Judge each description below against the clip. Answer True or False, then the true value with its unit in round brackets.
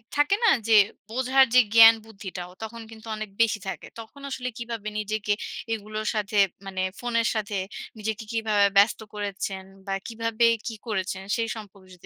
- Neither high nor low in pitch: False (220 Hz)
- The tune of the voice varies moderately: False (2.2 semitones)